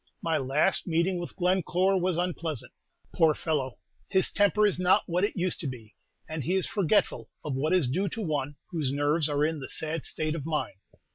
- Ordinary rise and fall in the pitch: Yes, average, 3.7 semitones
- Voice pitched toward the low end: No, medium, 165 Hz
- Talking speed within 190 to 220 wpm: Yes, average, 200 wpm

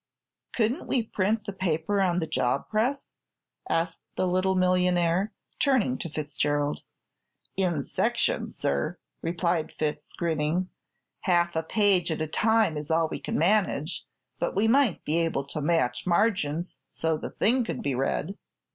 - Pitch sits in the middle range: Yes, medium, 175 Hz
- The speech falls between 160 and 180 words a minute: No, average, 150 wpm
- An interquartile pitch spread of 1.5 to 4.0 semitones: No, average, 4.4 semitones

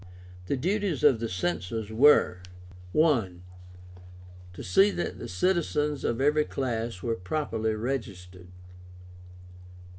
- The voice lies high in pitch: No, low, 120 Hz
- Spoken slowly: Yes, slow, 110 wpm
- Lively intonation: Yes, wide, 6.5 semitones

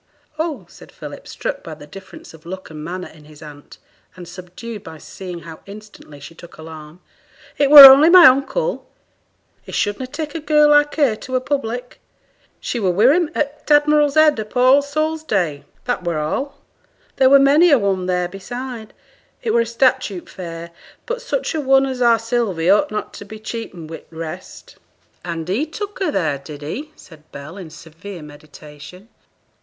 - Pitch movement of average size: No, wide, 8.7 semitones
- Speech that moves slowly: No, average, 185 wpm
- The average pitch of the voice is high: Yes, high, 215 Hz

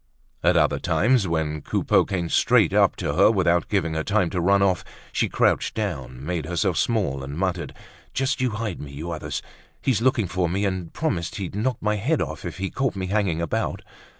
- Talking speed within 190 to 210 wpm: Yes, fast, 205 wpm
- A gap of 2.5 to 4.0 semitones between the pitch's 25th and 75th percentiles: No, average, 4.4 semitones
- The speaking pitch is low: Yes, very low, 95 Hz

